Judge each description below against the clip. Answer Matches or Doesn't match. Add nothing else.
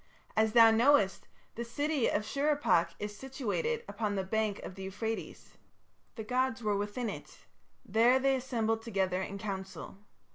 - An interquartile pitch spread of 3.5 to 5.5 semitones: Matches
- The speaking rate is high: Doesn't match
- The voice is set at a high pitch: Matches